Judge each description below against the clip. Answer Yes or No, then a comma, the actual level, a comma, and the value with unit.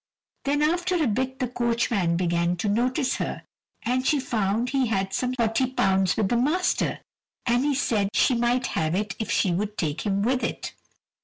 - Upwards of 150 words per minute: Yes, average, 180 wpm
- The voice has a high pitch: Yes, high, 235 Hz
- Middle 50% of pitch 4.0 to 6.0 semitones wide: Yes, average, 4.7 semitones